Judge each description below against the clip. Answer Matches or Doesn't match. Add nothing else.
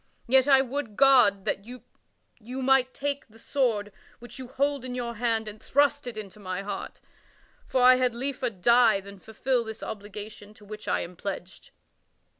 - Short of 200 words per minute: Matches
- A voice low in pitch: Doesn't match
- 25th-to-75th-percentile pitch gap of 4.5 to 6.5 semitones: Doesn't match